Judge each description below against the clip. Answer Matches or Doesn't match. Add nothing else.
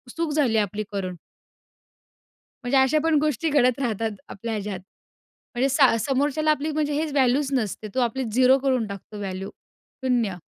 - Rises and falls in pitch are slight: Doesn't match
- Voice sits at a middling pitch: Doesn't match